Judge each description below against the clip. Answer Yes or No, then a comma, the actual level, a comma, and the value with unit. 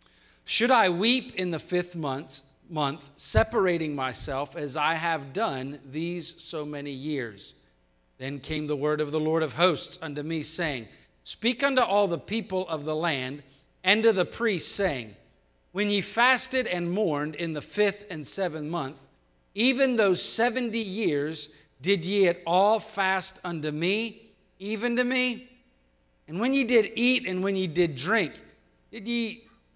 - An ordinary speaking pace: Yes, average, 160 wpm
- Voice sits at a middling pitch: Yes, medium, 175 Hz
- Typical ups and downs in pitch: No, wide, 6.3 semitones